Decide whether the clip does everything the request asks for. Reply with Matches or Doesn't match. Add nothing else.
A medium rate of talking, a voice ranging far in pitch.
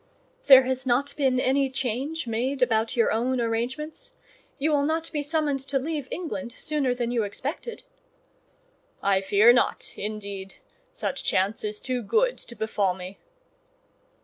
Doesn't match